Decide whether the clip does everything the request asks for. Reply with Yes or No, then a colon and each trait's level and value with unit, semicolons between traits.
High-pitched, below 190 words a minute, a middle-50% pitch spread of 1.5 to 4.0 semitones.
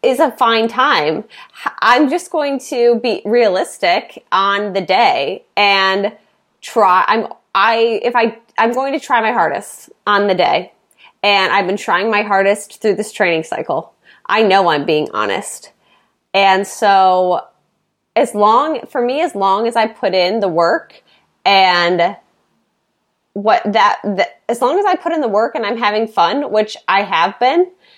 Yes: high, 210 Hz; average, 165 wpm; average, 3.7 semitones